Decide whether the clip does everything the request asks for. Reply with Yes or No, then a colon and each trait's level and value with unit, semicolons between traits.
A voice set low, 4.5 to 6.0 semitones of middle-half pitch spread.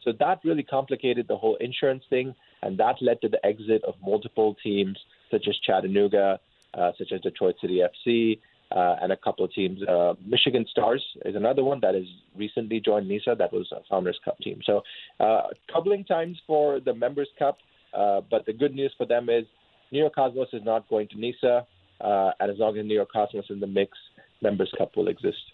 Yes: low, 115 Hz; average, 5.2 semitones